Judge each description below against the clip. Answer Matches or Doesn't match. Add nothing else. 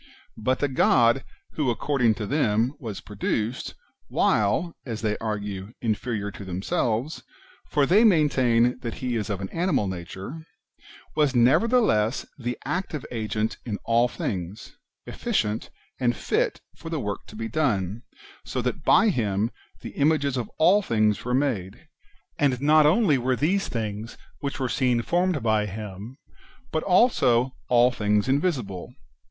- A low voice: Matches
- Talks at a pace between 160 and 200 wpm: Doesn't match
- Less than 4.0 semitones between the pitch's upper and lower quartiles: Doesn't match